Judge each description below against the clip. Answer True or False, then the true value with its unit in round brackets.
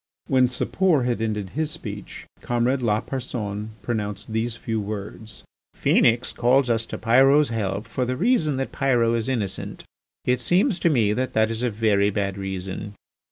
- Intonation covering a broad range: False (3.5 semitones)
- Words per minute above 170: False (160 wpm)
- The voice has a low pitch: True (115 Hz)